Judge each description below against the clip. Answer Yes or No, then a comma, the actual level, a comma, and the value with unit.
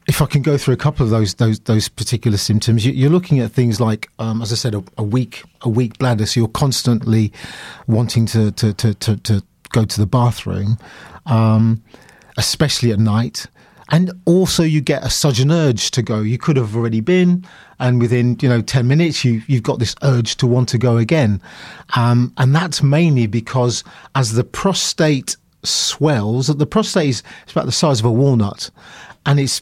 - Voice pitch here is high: No, low, 125 Hz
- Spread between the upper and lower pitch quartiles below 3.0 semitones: No, average, 4.2 semitones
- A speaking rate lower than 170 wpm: No, average, 195 wpm